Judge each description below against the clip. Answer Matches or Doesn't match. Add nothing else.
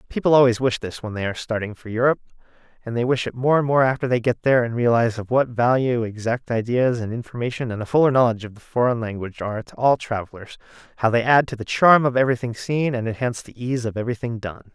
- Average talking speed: Doesn't match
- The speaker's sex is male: Matches